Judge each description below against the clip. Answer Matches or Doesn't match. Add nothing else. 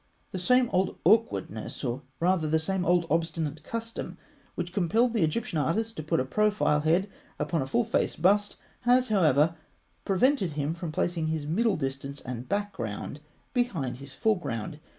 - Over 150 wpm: Matches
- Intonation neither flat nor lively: Doesn't match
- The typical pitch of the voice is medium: Matches